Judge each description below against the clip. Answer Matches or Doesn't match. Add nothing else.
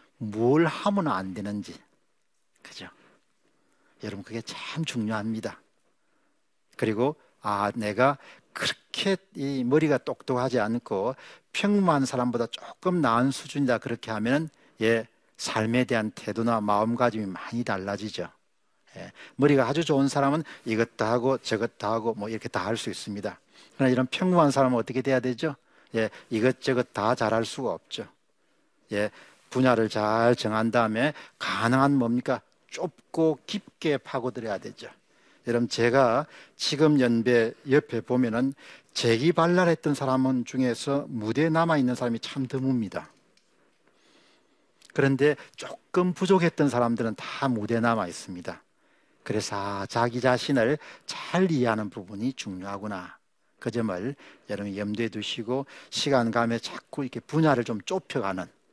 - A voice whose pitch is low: Matches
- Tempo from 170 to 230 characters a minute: Doesn't match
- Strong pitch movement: Doesn't match